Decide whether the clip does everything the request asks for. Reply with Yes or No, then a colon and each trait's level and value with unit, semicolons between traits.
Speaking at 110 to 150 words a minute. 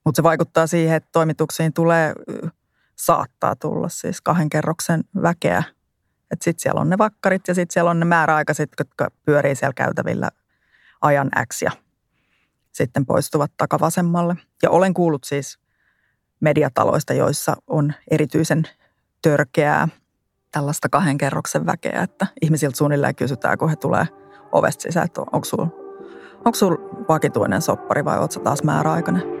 Yes: average, 135 wpm